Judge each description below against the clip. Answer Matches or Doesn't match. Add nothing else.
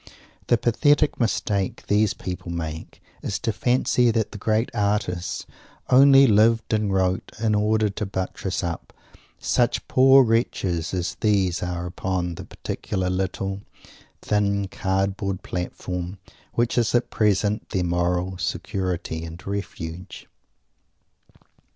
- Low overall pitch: Matches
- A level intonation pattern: Doesn't match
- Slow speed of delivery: Matches